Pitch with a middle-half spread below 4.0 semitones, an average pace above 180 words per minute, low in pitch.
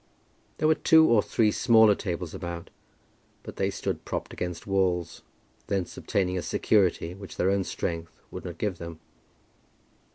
No: average, 3.3 semitones; average, 155 wpm; very low, 95 Hz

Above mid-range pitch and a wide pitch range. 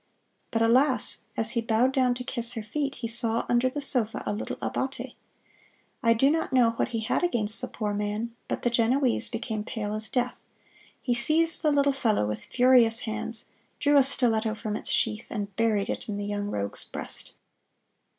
No: high, 230 Hz; average, 2.9 semitones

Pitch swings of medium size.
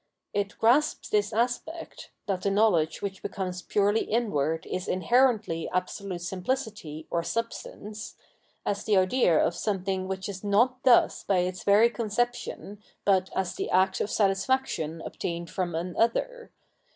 Yes: average, 3.9 semitones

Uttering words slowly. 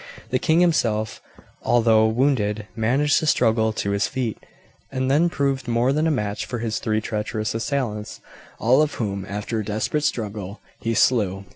No: average, 165 wpm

